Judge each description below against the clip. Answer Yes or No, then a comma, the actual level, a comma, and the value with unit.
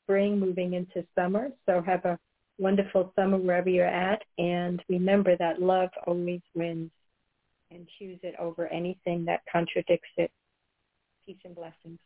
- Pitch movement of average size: No, narrow, 1.7 semitones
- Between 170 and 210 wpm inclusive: No, average, 145 wpm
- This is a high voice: No, medium, 175 Hz